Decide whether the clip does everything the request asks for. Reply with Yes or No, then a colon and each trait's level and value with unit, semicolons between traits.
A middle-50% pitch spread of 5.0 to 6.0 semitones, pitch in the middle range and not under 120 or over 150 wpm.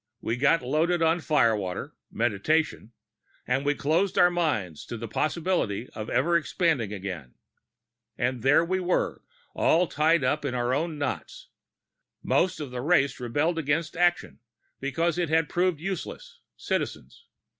Yes: wide, 5.5 semitones; medium, 150 Hz; average, 145 wpm